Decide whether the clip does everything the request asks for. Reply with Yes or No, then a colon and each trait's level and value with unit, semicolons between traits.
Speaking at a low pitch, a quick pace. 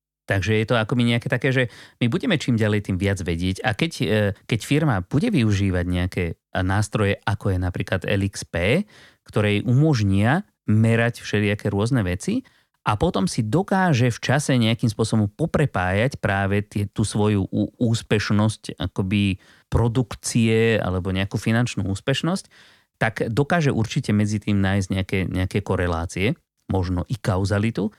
No: low, 105 Hz; average, 140 wpm